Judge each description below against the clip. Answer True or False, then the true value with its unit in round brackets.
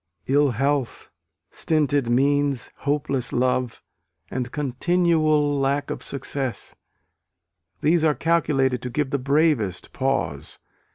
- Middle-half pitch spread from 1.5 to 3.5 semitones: True (2.6 semitones)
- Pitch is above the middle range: False (140 Hz)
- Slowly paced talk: True (105 wpm)